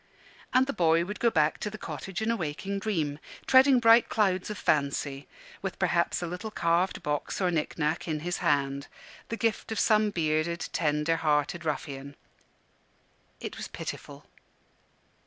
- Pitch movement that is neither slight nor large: No, wide, 5.8 semitones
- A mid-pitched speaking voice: Yes, medium, 170 Hz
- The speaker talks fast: No, average, 160 wpm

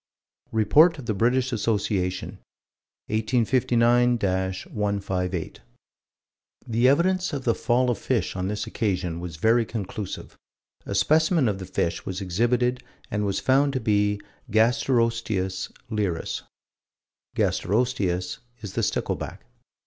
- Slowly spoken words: Yes, slow, 120 wpm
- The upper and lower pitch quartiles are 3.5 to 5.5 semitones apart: Yes, average, 4.5 semitones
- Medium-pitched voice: No, low, 110 Hz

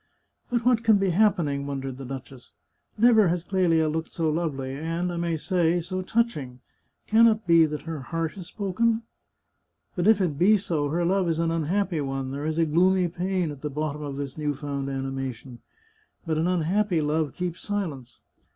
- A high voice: No, medium, 165 Hz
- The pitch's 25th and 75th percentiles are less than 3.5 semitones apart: No, average, 4.4 semitones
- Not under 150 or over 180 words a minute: No, average, 195 wpm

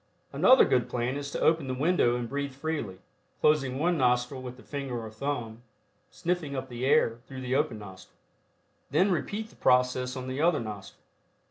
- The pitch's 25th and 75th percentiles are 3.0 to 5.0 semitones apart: Yes, average, 3.3 semitones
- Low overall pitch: Yes, low, 130 Hz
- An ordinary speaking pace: Yes, average, 180 wpm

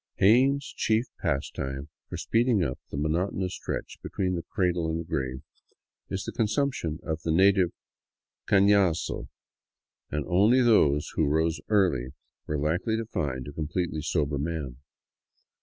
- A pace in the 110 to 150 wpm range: Yes, average, 140 wpm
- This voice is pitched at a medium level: No, very low, 85 Hz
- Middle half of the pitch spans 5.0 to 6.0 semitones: Yes, average, 5.3 semitones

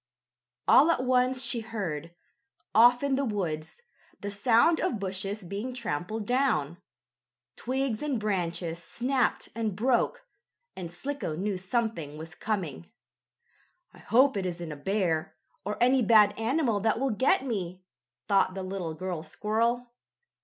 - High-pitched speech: Yes, high, 210 Hz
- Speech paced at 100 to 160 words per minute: Yes, average, 140 wpm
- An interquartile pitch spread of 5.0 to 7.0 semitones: Yes, wide, 5.4 semitones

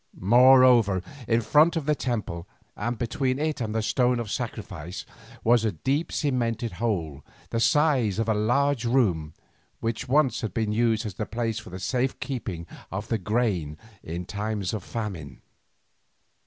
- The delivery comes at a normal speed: Yes, average, 155 wpm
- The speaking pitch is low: Yes, low, 115 Hz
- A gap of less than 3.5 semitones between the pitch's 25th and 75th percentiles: No, average, 4.0 semitones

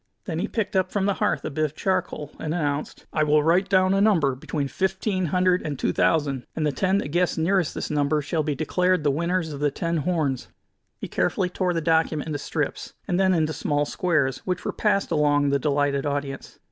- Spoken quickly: Yes, fast, 220 wpm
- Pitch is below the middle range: No, medium, 160 Hz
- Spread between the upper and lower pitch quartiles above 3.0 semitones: Yes, average, 4.1 semitones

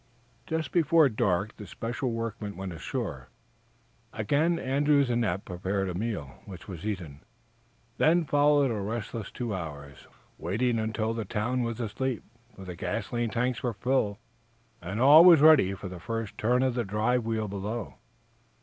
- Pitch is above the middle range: No, low, 115 Hz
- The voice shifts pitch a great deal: No, average, 4.5 semitones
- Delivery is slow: No, average, 160 wpm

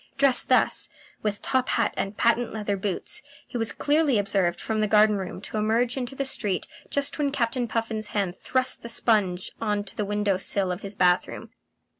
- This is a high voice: Yes, high, 215 Hz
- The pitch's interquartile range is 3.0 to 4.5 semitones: Yes, average, 3.4 semitones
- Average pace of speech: Yes, average, 195 wpm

